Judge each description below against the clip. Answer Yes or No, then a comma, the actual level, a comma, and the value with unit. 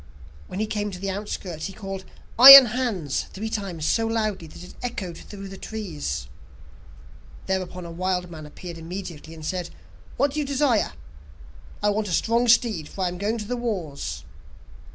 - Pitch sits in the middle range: No, high, 195 Hz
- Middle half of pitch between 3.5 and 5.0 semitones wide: Yes, average, 4.1 semitones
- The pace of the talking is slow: No, average, 175 wpm